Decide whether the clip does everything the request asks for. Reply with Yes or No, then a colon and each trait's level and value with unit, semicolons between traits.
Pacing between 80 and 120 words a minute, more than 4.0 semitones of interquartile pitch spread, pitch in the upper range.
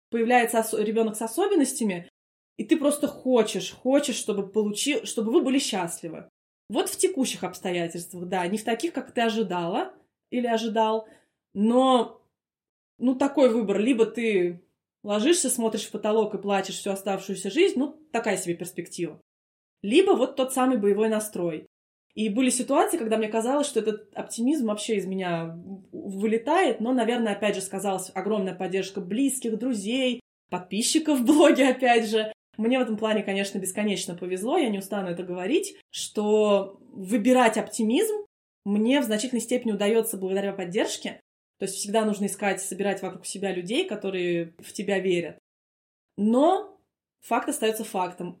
No: average, 150 wpm; average, 4.5 semitones; high, 215 Hz